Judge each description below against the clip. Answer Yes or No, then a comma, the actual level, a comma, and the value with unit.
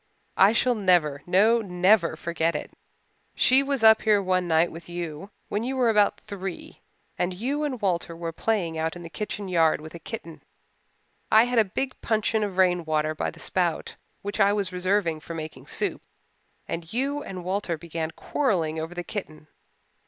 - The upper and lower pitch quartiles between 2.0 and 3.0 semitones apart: No, average, 4.5 semitones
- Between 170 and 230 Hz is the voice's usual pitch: Yes, medium, 185 Hz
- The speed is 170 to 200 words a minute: Yes, average, 180 wpm